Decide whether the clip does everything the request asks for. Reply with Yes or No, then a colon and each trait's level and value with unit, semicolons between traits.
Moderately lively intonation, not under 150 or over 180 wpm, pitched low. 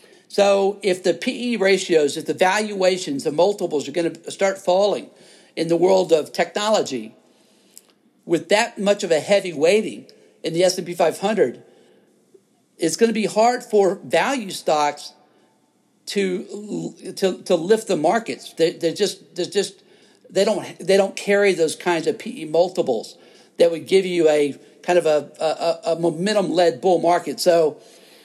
No: average, 3.3 semitones; average, 165 wpm; medium, 185 Hz